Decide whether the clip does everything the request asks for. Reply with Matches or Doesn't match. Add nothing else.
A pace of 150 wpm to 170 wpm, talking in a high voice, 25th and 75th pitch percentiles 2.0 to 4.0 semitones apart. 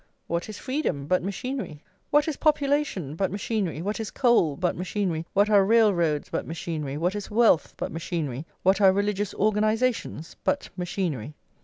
Doesn't match